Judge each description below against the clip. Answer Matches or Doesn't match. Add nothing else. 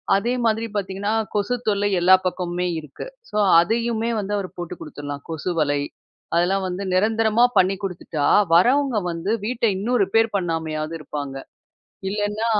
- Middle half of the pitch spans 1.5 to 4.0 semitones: Doesn't match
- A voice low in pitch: Doesn't match